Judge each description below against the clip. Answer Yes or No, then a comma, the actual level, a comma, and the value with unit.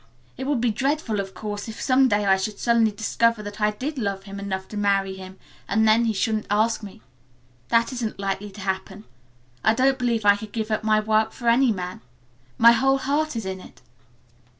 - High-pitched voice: Yes, high, 215 Hz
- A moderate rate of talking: No, fast, 210 wpm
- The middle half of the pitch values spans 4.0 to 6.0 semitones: No, average, 2.7 semitones